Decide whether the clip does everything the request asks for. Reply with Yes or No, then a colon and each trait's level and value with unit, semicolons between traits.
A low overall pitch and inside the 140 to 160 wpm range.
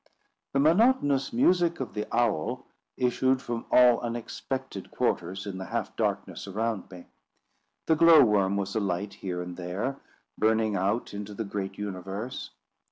Yes: low, 110 Hz; average, 145 wpm